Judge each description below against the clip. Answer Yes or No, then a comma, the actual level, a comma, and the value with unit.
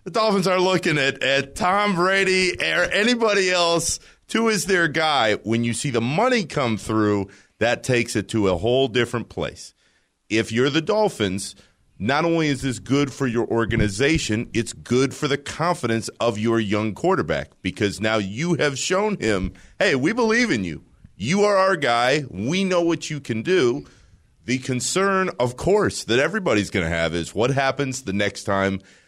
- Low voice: Yes, low, 130 Hz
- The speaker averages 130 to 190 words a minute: Yes, average, 180 wpm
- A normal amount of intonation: No, wide, 8.3 semitones